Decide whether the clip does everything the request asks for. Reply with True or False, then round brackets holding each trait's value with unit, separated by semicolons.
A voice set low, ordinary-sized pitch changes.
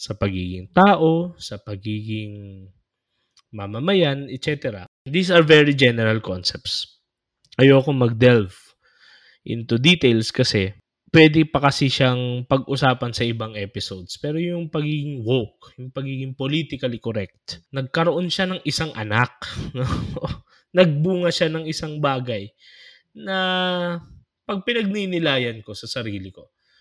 False (130 Hz; 6.4 semitones)